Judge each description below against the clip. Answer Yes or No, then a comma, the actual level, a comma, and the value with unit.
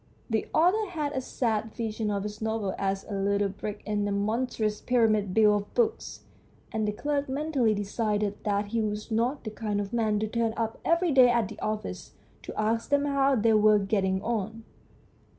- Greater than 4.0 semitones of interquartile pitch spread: No, average, 2.8 semitones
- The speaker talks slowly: No, average, 190 wpm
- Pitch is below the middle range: No, high, 220 Hz